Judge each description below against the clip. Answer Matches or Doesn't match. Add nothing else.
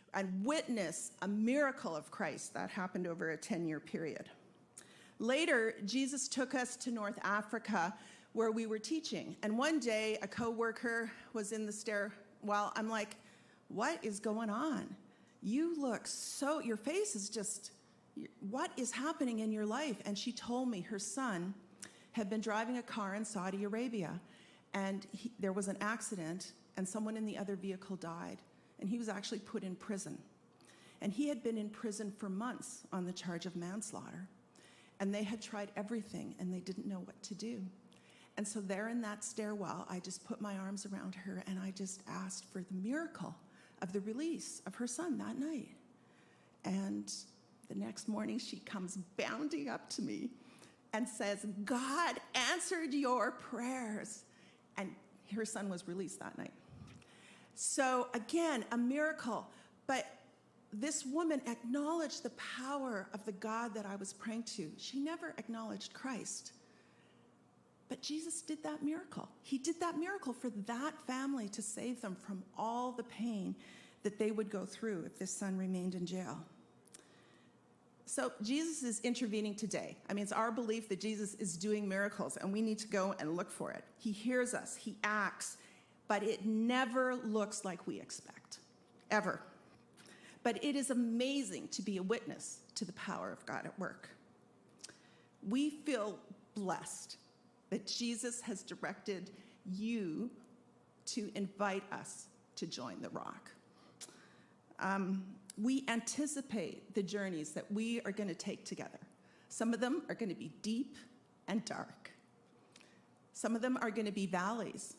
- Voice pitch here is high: Matches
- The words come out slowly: Doesn't match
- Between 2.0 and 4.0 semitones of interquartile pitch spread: Matches